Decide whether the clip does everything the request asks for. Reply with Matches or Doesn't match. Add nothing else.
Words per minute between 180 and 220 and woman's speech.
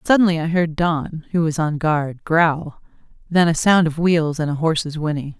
Matches